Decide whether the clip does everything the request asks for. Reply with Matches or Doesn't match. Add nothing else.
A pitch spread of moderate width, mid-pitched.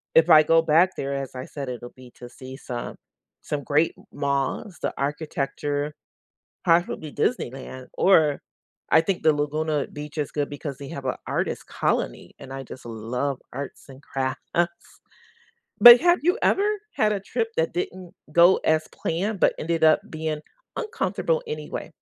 Matches